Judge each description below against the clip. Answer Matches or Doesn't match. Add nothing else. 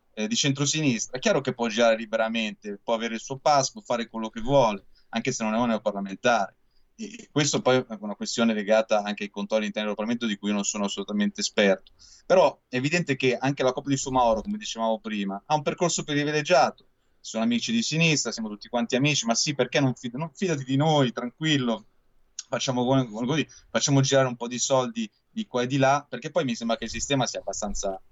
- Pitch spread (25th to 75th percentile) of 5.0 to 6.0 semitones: Doesn't match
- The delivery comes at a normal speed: Doesn't match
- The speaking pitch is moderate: Doesn't match